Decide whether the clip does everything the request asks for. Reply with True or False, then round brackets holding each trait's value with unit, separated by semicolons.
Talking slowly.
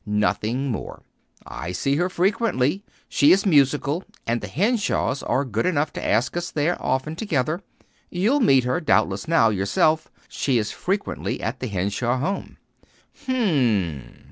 False (155 wpm)